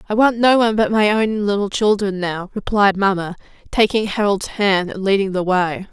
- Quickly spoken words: No, average, 195 wpm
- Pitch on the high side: Yes, high, 200 Hz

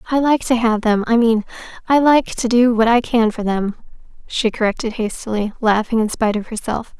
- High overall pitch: Yes, high, 230 Hz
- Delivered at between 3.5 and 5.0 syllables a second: No, 5.4 syllables/s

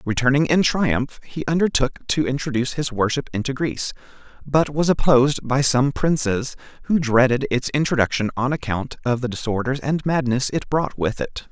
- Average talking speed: Yes, average, 165 wpm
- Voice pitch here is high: No, low, 135 Hz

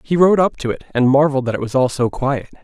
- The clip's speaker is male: Yes, male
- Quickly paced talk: Yes, fast, 295 wpm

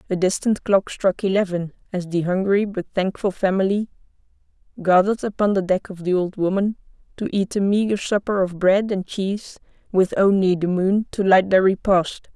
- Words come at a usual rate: Yes, average, 175 wpm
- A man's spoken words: No, female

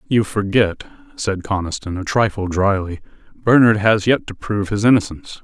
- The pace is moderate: Yes, average, 155 wpm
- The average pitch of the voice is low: Yes, low, 100 Hz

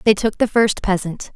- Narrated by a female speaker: Yes, female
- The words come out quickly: Yes, fast, 220 wpm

